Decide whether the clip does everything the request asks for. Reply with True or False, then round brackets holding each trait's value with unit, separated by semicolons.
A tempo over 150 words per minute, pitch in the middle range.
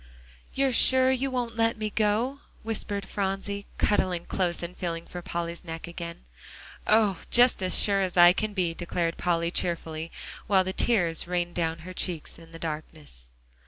True (165 wpm; 180 Hz)